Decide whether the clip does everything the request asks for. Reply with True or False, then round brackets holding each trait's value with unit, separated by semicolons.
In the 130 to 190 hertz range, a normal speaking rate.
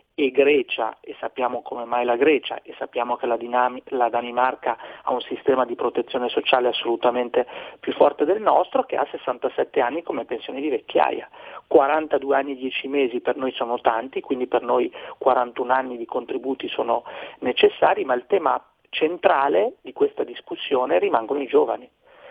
True (135 Hz; 160 wpm)